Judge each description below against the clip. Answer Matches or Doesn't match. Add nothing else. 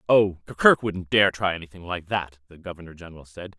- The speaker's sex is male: Matches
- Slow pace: Doesn't match